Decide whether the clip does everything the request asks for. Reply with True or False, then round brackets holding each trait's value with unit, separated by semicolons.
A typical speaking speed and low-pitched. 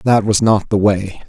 False (235 wpm; 100 Hz)